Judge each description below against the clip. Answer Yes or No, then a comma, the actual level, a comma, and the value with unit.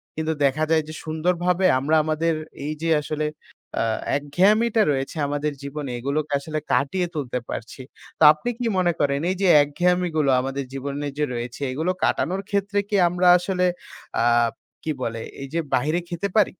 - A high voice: No, medium, 155 Hz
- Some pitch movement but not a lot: Yes, average, 4.2 semitones